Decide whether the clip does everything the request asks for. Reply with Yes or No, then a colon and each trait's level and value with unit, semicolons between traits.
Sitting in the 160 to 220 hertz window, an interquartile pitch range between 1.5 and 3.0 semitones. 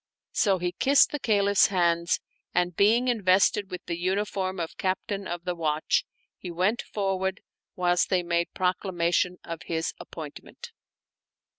Yes: medium, 185 Hz; narrow, 2.5 semitones